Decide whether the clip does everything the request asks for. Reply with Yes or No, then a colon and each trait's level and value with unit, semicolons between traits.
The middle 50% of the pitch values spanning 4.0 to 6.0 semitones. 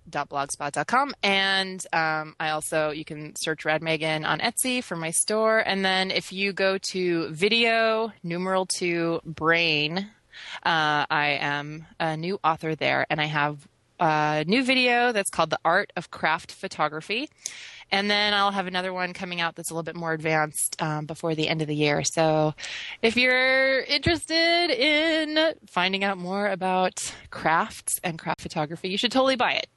Yes: average, 4.5 semitones